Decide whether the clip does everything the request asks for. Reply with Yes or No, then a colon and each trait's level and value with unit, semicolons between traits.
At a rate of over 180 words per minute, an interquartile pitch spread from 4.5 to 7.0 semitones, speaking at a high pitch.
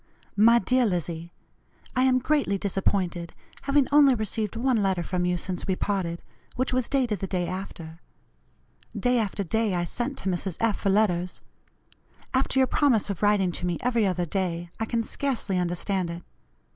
No: average, 170 wpm; average, 5.1 semitones; high, 200 Hz